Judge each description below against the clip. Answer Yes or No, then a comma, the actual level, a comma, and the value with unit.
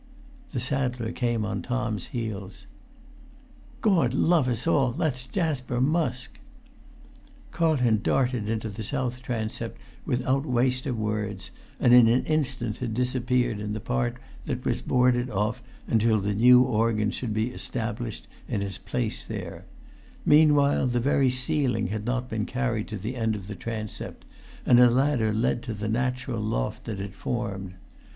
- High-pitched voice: No, low, 120 Hz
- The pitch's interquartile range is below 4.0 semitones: Yes, average, 2.9 semitones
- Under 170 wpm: Yes, average, 155 wpm